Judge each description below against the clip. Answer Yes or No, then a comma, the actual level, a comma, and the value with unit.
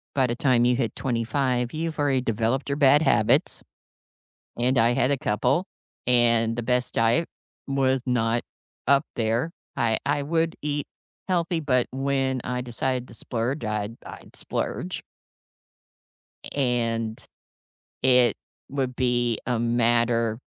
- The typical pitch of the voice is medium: No, low, 125 Hz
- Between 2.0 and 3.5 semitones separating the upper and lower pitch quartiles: Yes, average, 2.8 semitones